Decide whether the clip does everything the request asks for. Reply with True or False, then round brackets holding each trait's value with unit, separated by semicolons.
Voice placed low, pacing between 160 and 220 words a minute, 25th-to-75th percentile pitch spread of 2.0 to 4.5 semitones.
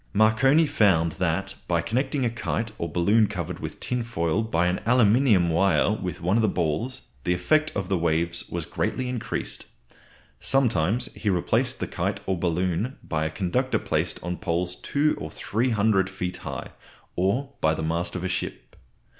False (95 Hz; 170 wpm; 5.1 semitones)